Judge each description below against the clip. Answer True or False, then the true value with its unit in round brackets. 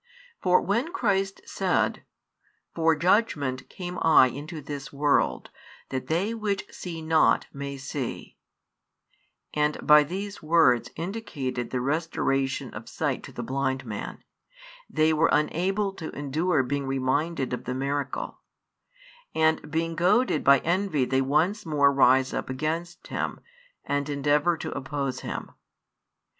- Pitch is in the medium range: True (150 Hz)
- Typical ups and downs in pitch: True (4.2 semitones)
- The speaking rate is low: True (130 wpm)